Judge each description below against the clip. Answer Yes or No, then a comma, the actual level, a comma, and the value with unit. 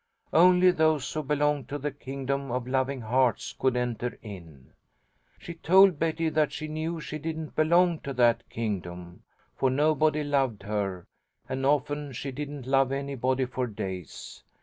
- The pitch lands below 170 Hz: Yes, medium, 140 Hz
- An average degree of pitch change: Yes, average, 3.9 semitones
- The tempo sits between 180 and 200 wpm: No, average, 150 wpm